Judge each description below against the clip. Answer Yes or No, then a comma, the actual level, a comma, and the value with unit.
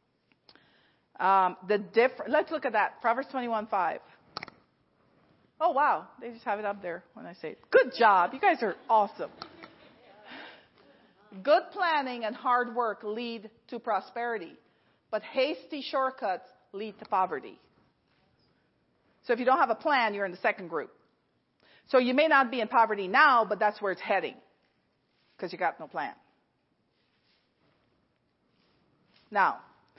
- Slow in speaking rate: No, average, 145 wpm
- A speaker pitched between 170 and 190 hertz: No, high, 230 Hz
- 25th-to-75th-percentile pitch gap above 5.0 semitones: No, average, 4.0 semitones